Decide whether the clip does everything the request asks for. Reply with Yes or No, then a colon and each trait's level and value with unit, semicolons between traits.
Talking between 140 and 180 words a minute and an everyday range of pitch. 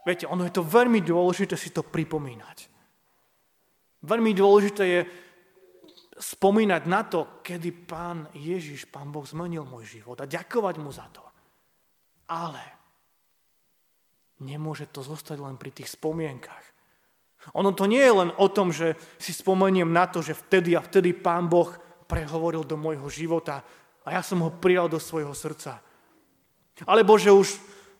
Yes: average, 150 wpm; average, 3.3 semitones